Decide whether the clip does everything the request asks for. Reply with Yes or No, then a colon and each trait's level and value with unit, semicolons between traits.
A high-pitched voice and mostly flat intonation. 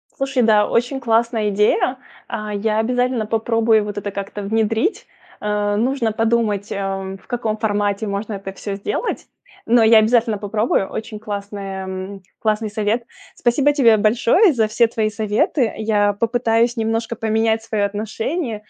Yes: high, 220 Hz; narrow, 2.1 semitones